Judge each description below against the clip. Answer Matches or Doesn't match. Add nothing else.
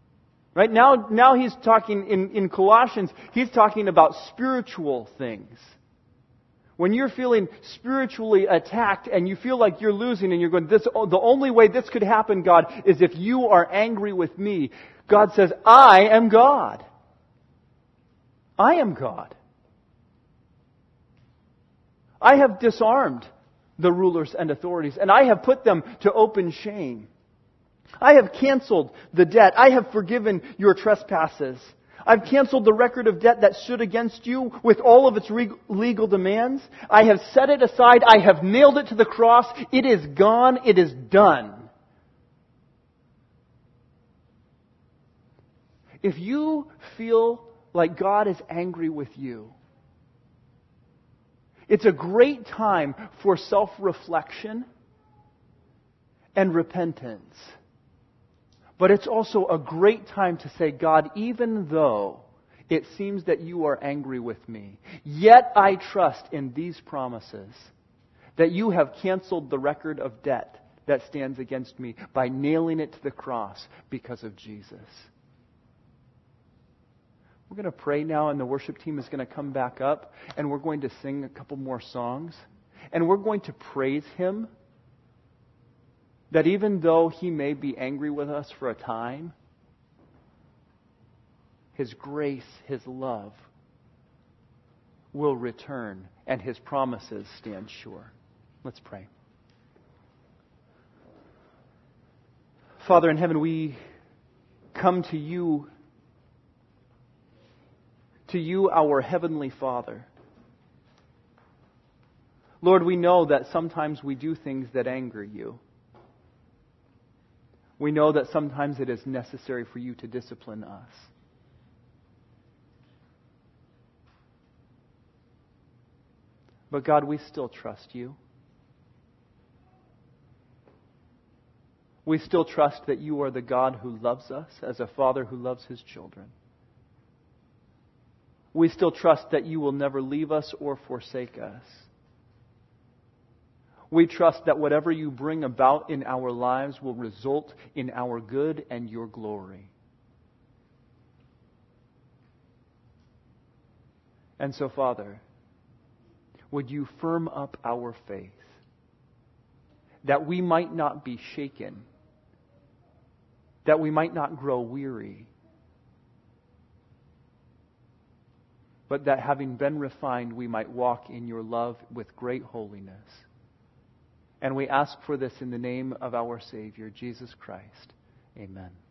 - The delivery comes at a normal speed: Doesn't match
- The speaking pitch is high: Doesn't match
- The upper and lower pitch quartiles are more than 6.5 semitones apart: Matches